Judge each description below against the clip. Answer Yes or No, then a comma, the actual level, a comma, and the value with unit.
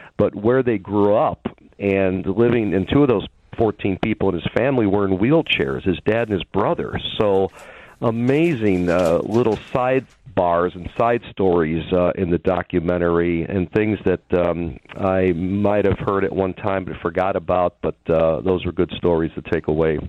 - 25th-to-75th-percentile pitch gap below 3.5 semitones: Yes, average, 2.9 semitones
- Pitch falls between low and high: No, very low, 95 Hz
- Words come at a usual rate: Yes, average, 175 wpm